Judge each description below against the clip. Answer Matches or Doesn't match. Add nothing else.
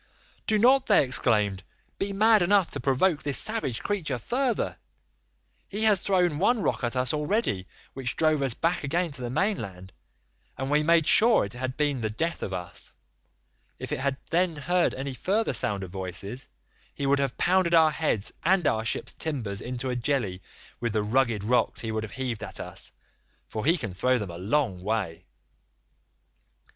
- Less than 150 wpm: Doesn't match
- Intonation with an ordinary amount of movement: Doesn't match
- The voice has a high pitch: Doesn't match